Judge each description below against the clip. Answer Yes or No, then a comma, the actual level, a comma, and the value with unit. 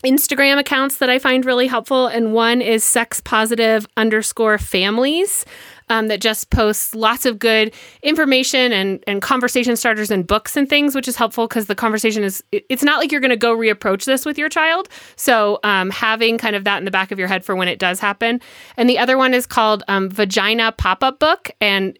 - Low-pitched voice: No, high, 230 Hz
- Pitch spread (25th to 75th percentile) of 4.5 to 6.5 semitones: No, average, 3.7 semitones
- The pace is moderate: No, fast, 210 wpm